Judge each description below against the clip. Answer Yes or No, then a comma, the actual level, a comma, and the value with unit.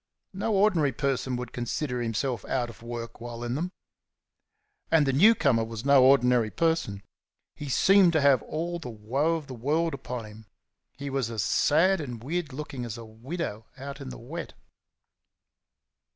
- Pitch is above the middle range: No, low, 135 Hz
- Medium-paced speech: Yes, average, 170 wpm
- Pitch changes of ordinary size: Yes, average, 4.9 semitones